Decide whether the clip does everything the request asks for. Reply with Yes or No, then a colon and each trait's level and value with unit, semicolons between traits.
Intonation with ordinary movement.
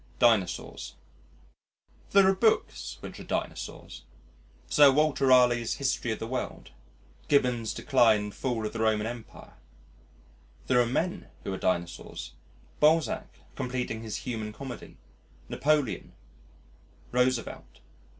Yes: average, 3.5 semitones